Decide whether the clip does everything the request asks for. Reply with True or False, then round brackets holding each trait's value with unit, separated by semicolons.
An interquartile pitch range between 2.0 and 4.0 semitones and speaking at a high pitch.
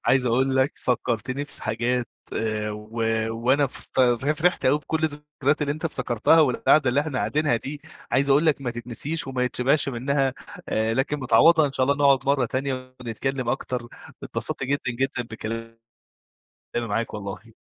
False (3.2 semitones; 130 Hz)